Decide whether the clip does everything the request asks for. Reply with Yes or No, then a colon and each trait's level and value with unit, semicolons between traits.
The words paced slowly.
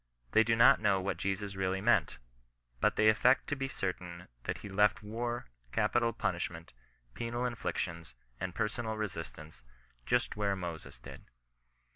No: average, 150 wpm